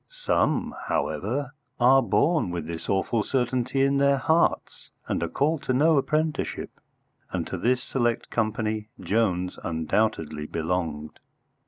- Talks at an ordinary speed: No, slow, 130 wpm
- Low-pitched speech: Yes, low, 120 Hz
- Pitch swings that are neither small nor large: No, wide, 7.2 semitones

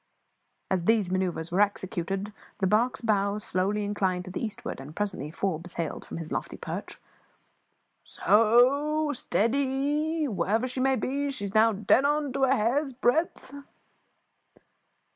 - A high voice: Yes, high, 215 Hz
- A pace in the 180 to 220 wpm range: No, average, 155 wpm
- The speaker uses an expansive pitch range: Yes, wide, 5.9 semitones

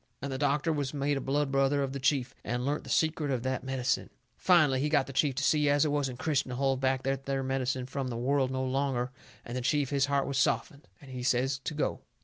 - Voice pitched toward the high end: No, low, 135 Hz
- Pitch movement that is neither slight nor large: No, narrow, 1.6 semitones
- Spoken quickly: Yes, fast, 255 wpm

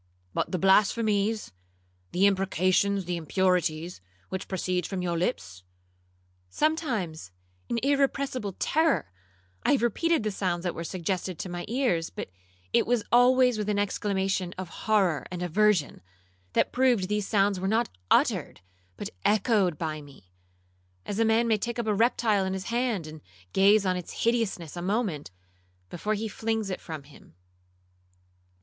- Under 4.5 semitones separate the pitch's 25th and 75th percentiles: No, average, 4.8 semitones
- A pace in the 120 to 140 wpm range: No, average, 150 wpm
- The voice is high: Yes, high, 195 Hz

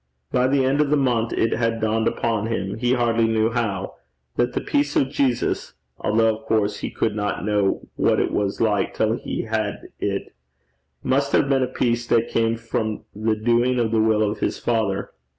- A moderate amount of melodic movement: No, narrow, 2.2 semitones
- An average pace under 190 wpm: No, average, 200 wpm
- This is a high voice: No, low, 115 Hz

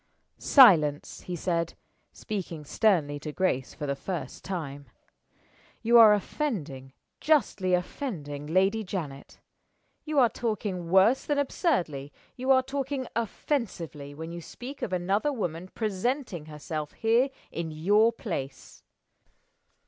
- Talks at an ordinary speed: No, slow, 120 wpm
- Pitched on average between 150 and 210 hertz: Yes, medium, 185 Hz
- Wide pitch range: Yes, wide, 7.3 semitones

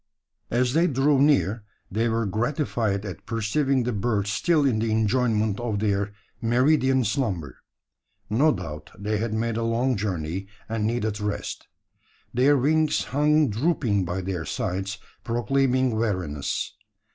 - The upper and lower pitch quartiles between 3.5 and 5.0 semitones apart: Yes, average, 4.4 semitones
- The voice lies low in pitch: Yes, low, 115 Hz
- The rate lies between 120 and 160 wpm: Yes, slow, 135 wpm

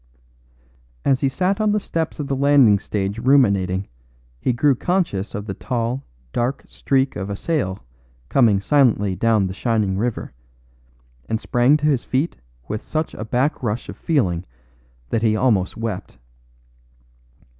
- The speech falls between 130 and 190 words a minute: Yes, average, 145 wpm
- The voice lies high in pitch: No, low, 120 Hz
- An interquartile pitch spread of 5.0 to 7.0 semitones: Yes, wide, 5.4 semitones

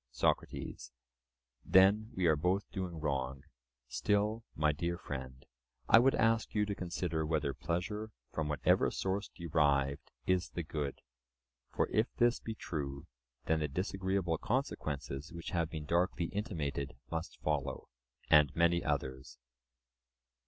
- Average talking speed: No, slow, 130 wpm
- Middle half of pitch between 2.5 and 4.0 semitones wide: No, average, 4.7 semitones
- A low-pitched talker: Yes, very low, 85 Hz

